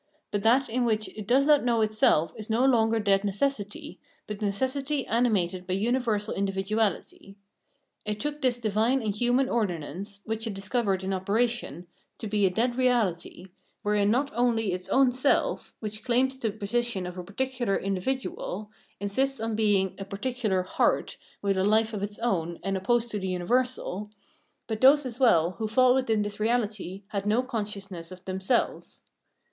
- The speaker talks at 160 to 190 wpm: Yes, average, 175 wpm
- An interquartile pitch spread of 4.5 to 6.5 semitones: No, average, 3.8 semitones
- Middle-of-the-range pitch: No, high, 215 Hz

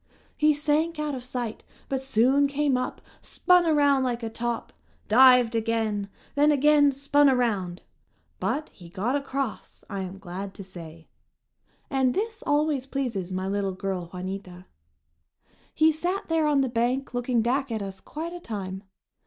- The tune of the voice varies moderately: No, wide, 6.4 semitones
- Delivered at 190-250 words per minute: No, average, 155 wpm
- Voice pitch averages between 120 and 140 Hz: No, very high, 250 Hz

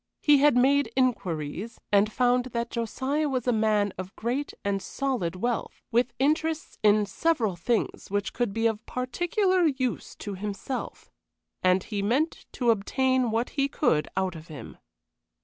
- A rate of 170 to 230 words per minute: No, average, 155 wpm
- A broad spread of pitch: No, average, 4.7 semitones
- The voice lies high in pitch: Yes, high, 235 Hz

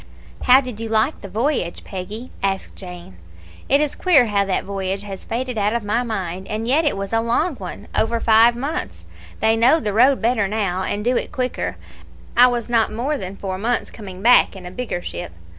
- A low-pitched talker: No, high, 220 Hz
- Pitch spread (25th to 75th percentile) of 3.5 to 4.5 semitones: Yes, average, 4.0 semitones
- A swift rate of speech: Yes, fast, 210 wpm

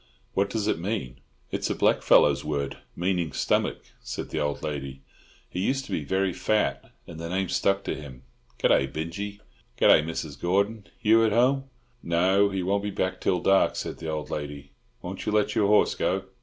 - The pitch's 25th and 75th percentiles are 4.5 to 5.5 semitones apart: Yes, average, 5.0 semitones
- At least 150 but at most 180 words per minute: No, average, 195 wpm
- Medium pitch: No, very low, 95 Hz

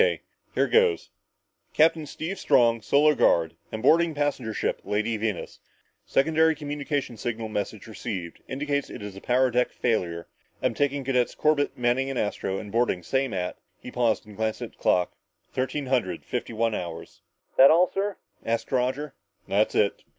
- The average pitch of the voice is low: Yes, low, 125 Hz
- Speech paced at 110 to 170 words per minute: Yes, average, 165 wpm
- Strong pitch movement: No, average, 5.0 semitones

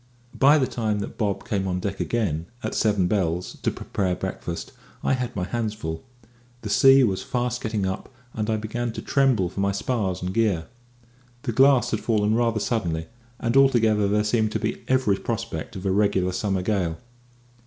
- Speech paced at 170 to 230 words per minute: Yes, average, 185 wpm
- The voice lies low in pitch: Yes, low, 105 Hz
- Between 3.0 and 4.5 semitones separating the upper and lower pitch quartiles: Yes, average, 3.7 semitones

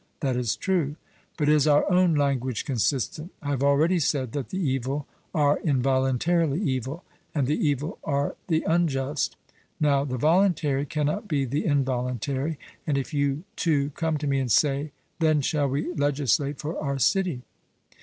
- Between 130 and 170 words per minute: Yes, average, 160 wpm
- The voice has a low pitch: No, medium, 145 Hz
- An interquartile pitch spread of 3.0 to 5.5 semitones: No, narrow, 2.5 semitones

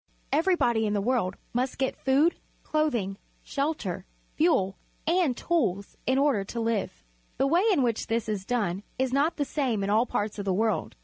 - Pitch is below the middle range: No, high, 240 Hz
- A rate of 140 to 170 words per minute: No, average, 180 wpm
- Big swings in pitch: Yes, wide, 5.8 semitones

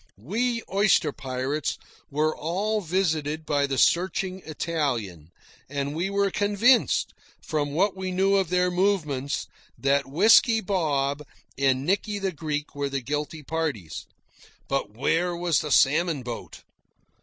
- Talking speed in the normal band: No, slow, 130 wpm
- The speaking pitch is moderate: Yes, medium, 160 Hz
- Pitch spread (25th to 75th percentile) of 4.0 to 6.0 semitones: Yes, average, 5.1 semitones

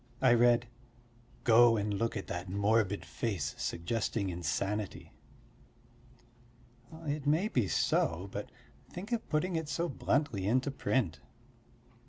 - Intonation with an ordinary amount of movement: No, wide, 6.2 semitones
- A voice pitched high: No, low, 115 Hz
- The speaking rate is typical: No, slow, 120 wpm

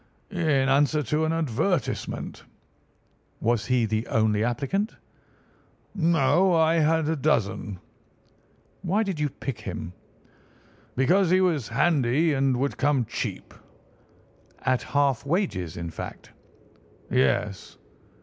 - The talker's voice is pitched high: No, medium, 140 Hz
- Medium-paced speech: No, slow, 110 wpm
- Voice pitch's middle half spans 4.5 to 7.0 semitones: Yes, wide, 5.5 semitones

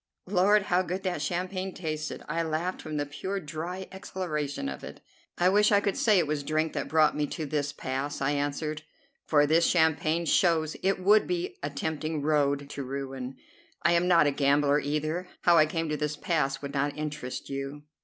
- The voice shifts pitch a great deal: No, average, 3.4 semitones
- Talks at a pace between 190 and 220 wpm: Yes, average, 195 wpm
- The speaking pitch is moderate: Yes, medium, 155 Hz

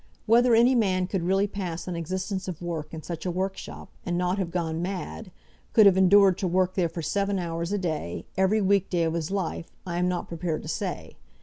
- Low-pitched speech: No, medium, 185 Hz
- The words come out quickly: Yes, fast, 220 wpm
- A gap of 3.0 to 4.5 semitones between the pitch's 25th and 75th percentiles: No, narrow, 2.6 semitones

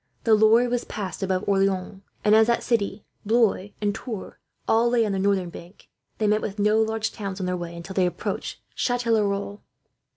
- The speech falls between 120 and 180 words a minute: No, average, 190 wpm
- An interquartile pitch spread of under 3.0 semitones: Yes, narrow, 2.4 semitones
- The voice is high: Yes, high, 205 Hz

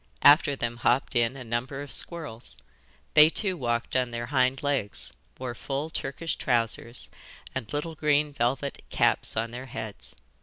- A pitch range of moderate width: Yes, average, 3.5 semitones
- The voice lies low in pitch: Yes, low, 130 Hz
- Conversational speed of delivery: Yes, average, 155 wpm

